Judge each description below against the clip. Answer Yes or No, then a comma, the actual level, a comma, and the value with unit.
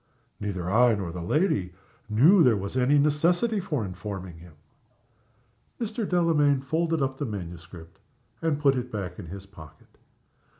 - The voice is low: Yes, low, 125 Hz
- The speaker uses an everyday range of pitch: No, wide, 8.6 semitones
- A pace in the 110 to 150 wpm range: Yes, average, 145 wpm